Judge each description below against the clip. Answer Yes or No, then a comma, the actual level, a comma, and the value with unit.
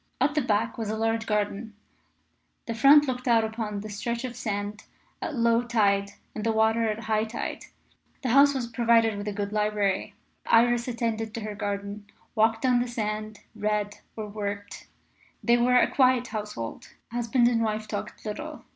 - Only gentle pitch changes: Yes, narrow, 2.2 semitones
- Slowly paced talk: No, average, 175 wpm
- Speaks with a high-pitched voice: Yes, high, 220 Hz